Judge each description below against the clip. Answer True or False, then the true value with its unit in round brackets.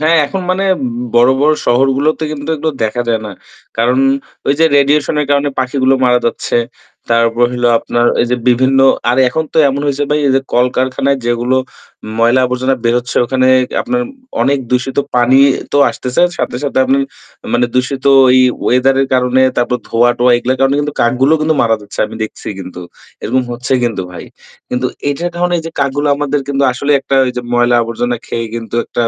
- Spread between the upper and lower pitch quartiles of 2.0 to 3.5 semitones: True (2.6 semitones)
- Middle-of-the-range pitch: False (130 Hz)